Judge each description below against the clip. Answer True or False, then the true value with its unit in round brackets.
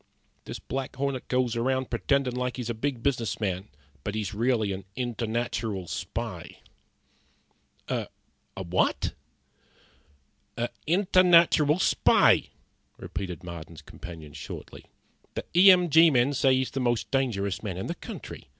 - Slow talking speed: True (130 wpm)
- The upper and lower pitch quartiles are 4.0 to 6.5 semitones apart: True (5.1 semitones)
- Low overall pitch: True (120 Hz)